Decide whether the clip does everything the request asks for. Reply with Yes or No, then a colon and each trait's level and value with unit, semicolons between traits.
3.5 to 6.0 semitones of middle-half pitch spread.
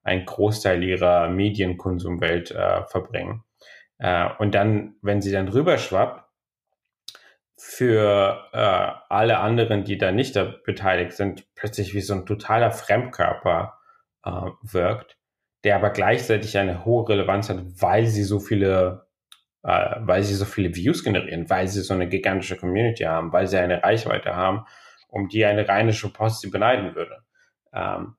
No: narrow, 2.5 semitones